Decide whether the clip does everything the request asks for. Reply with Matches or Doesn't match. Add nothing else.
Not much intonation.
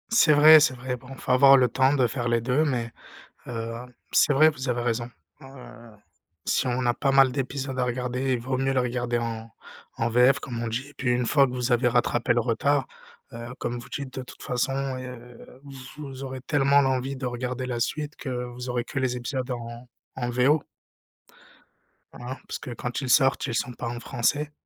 Matches